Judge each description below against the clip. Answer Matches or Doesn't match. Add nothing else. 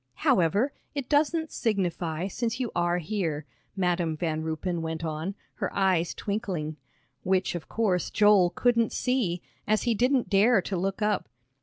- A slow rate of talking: Doesn't match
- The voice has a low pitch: Doesn't match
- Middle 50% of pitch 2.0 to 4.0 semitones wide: Doesn't match